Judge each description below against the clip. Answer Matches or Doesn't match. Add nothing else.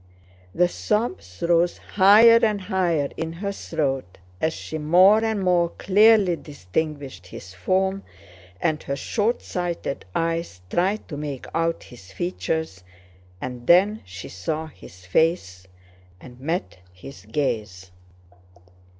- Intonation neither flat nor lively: Doesn't match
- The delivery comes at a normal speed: Doesn't match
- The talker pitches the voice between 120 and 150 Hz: Doesn't match